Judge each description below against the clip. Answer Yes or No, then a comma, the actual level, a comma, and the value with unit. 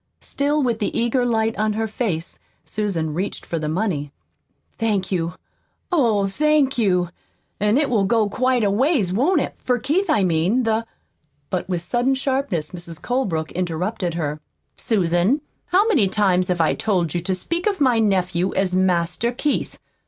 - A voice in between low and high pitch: No, high, 205 Hz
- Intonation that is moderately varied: No, wide, 5.8 semitones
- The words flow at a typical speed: Yes, average, 170 wpm